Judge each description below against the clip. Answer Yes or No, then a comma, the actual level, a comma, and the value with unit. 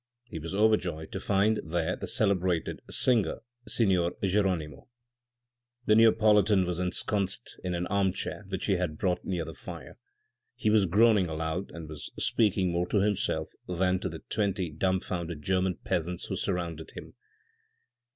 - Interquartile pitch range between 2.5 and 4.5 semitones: Yes, average, 2.8 semitones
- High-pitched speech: No, very low, 95 Hz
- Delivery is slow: No, average, 150 wpm